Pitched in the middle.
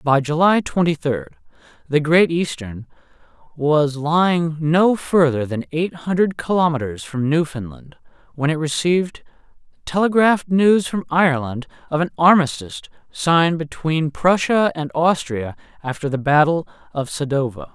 Yes: medium, 155 Hz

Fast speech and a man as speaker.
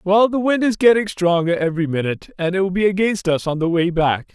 Yes: fast, 250 wpm; male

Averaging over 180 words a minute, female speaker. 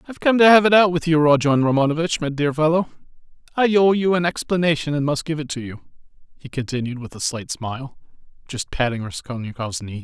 No: fast, 205 wpm; male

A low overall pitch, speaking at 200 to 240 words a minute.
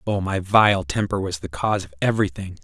Yes: very low, 95 Hz; fast, 205 wpm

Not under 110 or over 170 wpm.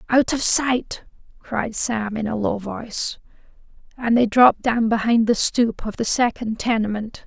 Yes: average, 165 wpm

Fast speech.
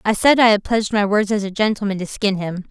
Yes: fast, 290 wpm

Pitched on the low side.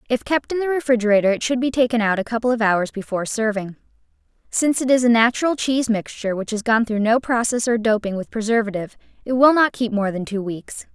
No: high, 230 Hz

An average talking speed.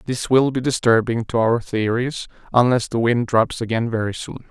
Yes: average, 185 wpm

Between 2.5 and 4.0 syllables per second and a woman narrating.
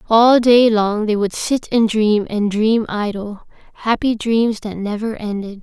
Yes: 3.9 syllables/s; female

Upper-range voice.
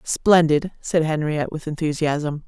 No: medium, 155 Hz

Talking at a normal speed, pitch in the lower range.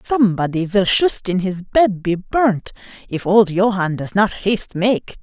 No: average, 170 wpm; high, 195 Hz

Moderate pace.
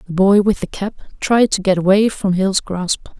No: fast, 225 wpm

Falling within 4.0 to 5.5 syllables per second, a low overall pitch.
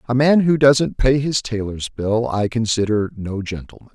Yes: 4.6 syllables/s; low, 120 Hz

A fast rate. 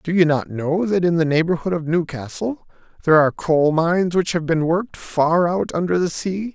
Yes: fast, 210 wpm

